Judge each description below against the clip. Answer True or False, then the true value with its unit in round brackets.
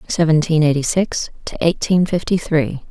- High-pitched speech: False (160 Hz)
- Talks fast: False (145 wpm)